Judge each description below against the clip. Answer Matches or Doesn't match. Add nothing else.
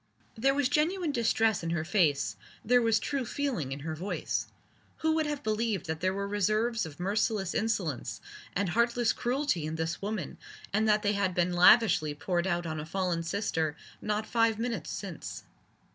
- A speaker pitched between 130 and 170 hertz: Doesn't match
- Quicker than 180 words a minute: Doesn't match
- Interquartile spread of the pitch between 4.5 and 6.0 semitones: Matches